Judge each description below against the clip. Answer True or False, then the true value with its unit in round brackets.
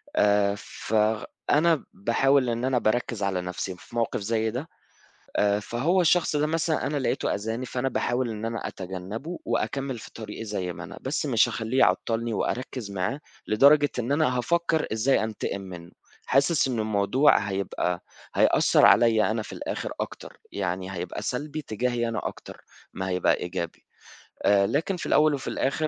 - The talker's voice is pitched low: True (115 Hz)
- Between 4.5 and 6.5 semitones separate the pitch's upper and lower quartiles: True (5.1 semitones)